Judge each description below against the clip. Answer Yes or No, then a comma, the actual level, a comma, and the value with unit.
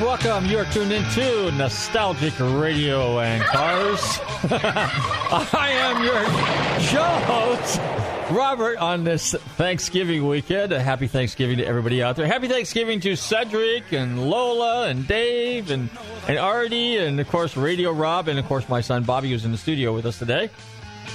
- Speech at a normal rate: Yes, average, 155 wpm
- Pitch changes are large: Yes, wide, 8.6 semitones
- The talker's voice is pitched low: No, medium, 155 Hz